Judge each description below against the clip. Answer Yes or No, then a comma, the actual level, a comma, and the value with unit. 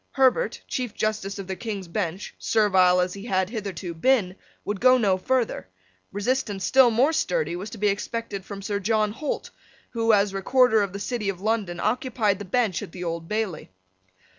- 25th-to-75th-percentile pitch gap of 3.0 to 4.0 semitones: Yes, average, 3.5 semitones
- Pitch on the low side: No, high, 205 Hz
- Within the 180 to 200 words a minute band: Yes, average, 185 wpm